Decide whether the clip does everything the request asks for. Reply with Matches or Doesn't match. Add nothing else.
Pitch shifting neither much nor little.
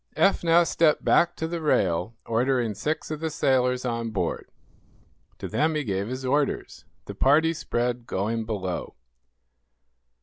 Doesn't match